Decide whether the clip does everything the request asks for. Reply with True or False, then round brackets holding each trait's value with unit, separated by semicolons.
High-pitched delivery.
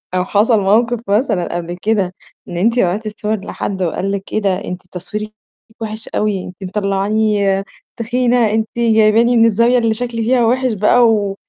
True (215 Hz)